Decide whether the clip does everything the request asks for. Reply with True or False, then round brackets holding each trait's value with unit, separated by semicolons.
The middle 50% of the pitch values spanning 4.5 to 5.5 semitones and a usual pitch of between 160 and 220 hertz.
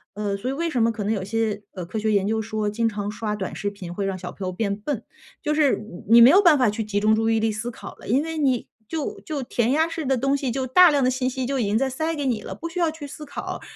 False (5.0 semitones; 230 Hz)